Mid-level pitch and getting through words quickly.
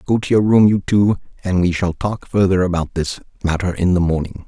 No: very low, 95 Hz; fast, 230 wpm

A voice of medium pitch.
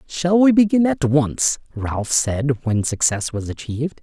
Yes: medium, 145 Hz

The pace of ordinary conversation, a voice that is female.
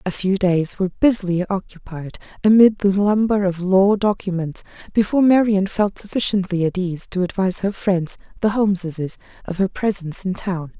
Yes: average, 160 wpm; female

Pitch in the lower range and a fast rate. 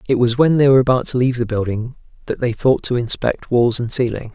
Yes: low, 125 Hz; fast, 250 wpm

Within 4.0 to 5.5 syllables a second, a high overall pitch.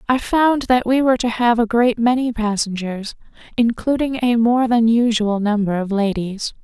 Yes: 4.7 syllables/s; high, 230 Hz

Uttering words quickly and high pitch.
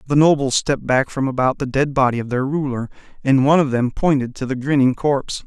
No: fast, 230 wpm; low, 135 Hz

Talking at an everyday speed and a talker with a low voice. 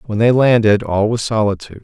Yes: average, 195 wpm; low, 110 Hz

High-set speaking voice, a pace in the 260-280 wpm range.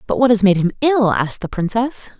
No: high, 215 Hz; fast, 245 wpm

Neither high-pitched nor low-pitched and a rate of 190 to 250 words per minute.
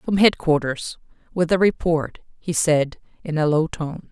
No: medium, 165 Hz; average, 145 wpm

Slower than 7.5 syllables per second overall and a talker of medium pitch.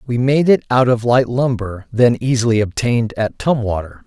No: 5.1 syllables/s; low, 120 Hz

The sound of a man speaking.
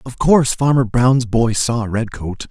Yes: male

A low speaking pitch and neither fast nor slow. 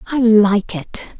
No: high, 215 Hz; average, 150 wpm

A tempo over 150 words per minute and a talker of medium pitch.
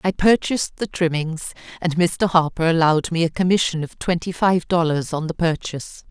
Yes: average, 175 wpm; medium, 170 Hz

